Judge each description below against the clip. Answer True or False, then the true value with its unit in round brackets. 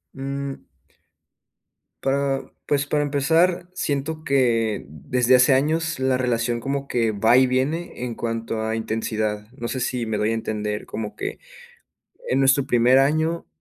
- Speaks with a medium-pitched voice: False (130 Hz)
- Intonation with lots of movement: False (3.6 semitones)